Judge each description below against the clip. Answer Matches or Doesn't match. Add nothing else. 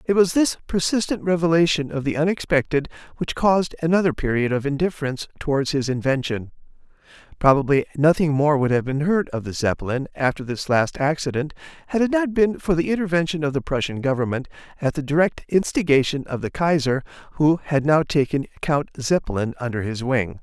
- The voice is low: Doesn't match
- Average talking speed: Matches